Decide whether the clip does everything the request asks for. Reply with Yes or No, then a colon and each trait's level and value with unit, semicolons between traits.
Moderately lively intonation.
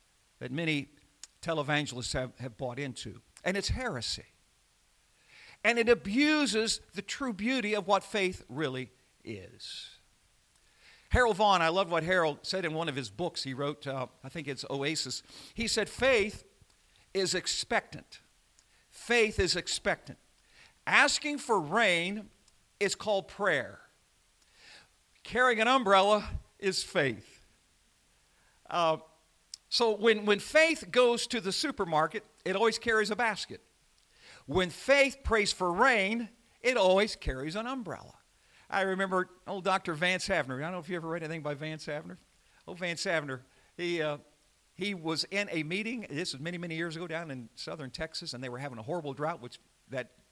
No: wide, 6.5 semitones